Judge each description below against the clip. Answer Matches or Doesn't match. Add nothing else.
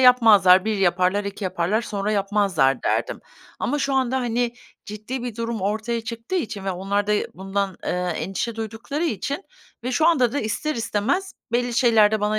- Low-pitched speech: Doesn't match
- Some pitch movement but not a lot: Matches